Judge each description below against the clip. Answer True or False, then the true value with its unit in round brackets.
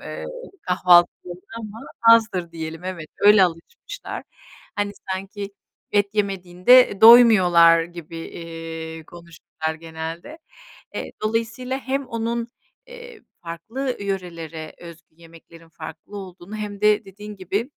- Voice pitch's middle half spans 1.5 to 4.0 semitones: False (4.6 semitones)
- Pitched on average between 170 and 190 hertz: True (185 Hz)